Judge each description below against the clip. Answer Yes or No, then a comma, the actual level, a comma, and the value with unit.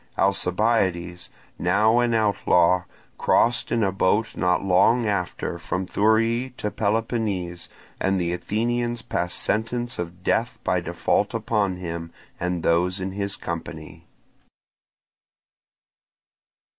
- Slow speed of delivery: Yes, slow, 110 wpm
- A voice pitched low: Yes, low, 100 Hz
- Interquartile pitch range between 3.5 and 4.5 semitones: Yes, average, 4.1 semitones